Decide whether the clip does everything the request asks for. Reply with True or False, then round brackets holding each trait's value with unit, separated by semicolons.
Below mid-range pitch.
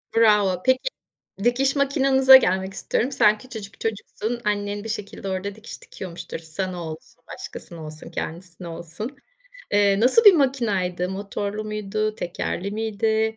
False (210 Hz)